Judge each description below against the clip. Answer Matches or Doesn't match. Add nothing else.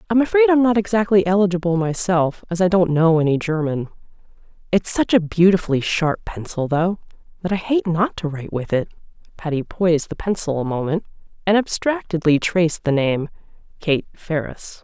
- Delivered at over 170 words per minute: Doesn't match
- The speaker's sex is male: Doesn't match